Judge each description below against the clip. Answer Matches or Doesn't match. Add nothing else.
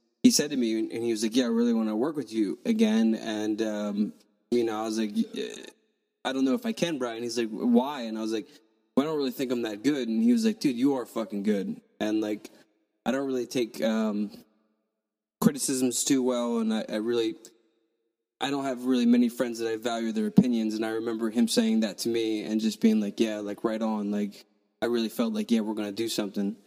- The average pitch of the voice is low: Matches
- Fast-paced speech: Matches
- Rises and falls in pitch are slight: Doesn't match